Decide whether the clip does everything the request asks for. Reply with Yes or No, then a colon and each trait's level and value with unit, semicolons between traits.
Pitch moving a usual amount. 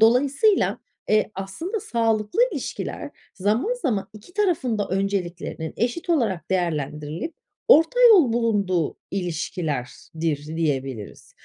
No: wide, 8.4 semitones